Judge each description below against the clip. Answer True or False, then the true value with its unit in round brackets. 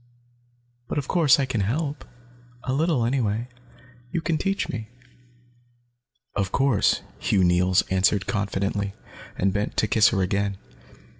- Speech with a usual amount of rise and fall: False (5.9 semitones)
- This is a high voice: False (105 Hz)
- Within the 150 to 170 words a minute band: False (135 wpm)